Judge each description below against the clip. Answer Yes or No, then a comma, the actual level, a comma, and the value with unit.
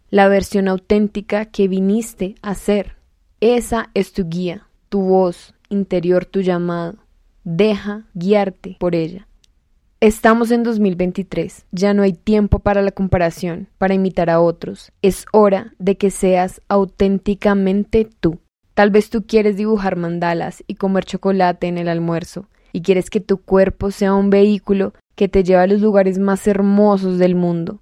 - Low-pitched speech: No, high, 195 Hz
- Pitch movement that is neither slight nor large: No, narrow, 2.1 semitones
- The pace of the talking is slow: No, average, 155 wpm